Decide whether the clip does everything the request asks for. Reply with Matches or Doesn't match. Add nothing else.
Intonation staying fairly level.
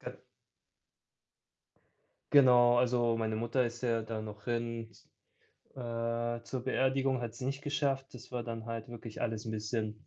Matches